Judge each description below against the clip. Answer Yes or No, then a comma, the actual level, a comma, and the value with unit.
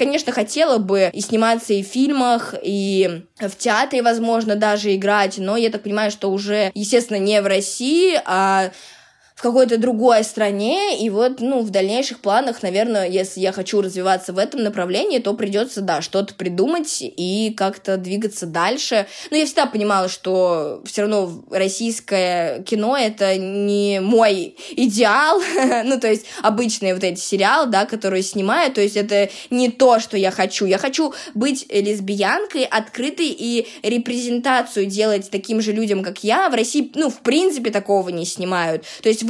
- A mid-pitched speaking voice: No, high, 210 Hz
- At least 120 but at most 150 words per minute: No, fast, 160 wpm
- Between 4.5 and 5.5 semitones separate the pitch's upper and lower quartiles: No, average, 3.7 semitones